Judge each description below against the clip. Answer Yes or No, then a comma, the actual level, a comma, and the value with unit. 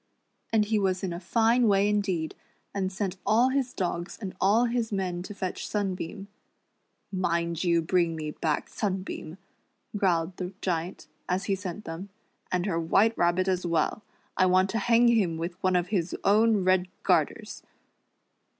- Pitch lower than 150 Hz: No, medium, 185 Hz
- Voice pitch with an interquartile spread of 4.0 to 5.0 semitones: No, average, 3.0 semitones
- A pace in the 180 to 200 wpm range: No, average, 165 wpm